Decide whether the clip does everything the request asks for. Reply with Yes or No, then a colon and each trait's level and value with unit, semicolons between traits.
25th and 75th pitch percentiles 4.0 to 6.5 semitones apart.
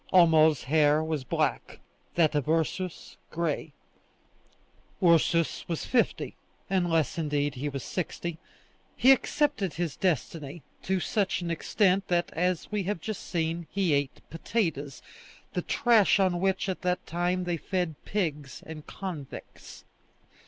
No: average, 3.4 semitones